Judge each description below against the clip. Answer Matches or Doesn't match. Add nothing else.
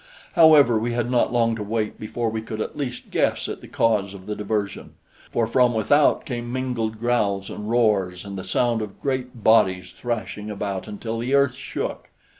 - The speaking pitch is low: Matches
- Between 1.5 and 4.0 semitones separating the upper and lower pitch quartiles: Matches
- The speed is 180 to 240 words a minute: Matches